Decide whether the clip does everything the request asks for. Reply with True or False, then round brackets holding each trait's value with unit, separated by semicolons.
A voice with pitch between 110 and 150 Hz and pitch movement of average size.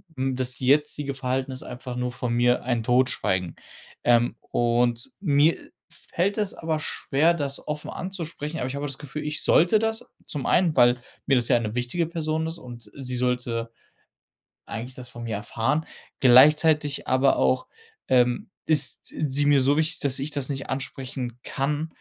True (135 Hz; 3.7 semitones)